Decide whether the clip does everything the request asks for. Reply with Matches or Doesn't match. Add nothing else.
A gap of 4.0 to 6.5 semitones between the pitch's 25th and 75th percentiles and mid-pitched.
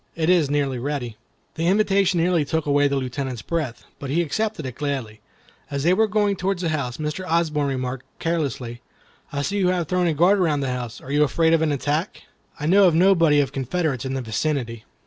Matches